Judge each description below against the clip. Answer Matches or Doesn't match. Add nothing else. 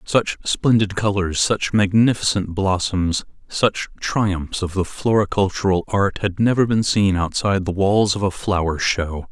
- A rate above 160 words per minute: Doesn't match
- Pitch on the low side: Matches